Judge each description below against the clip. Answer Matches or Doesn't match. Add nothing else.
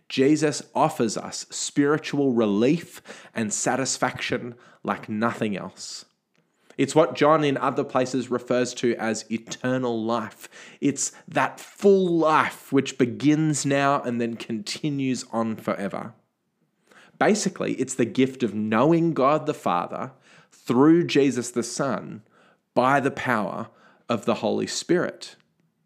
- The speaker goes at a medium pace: Doesn't match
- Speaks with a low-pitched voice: Matches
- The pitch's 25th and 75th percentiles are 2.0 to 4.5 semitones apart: Matches